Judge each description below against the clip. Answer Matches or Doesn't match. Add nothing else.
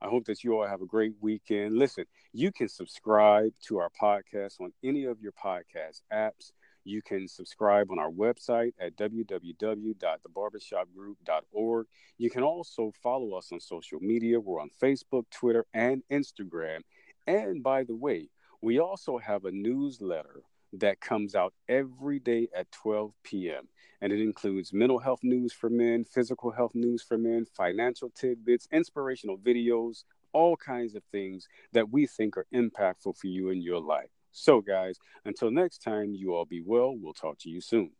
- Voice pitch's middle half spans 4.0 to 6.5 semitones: Doesn't match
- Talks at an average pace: Matches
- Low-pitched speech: Matches